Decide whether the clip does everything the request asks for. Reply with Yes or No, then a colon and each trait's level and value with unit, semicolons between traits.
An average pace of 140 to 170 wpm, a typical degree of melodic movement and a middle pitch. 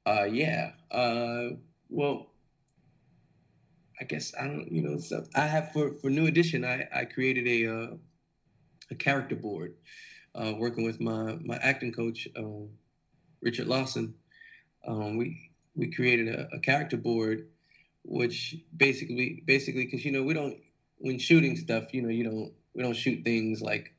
No: average, 160 wpm; average, 3.9 semitones; low, 125 Hz